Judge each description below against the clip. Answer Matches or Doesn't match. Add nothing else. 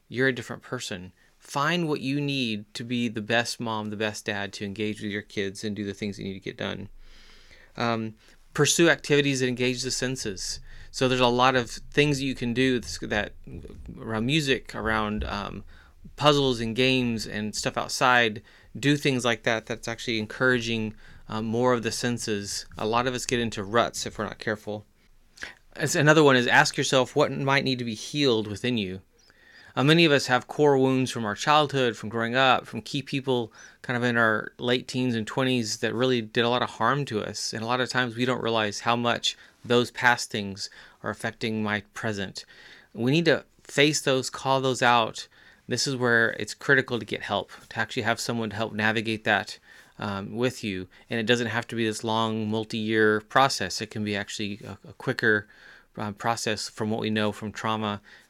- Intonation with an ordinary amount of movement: Matches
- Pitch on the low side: Matches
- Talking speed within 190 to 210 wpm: Matches